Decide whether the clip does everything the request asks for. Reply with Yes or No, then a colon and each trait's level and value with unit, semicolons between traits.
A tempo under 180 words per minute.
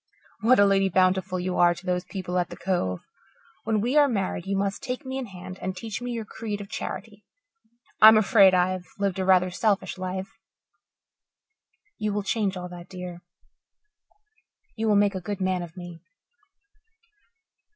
Yes: average, 170 wpm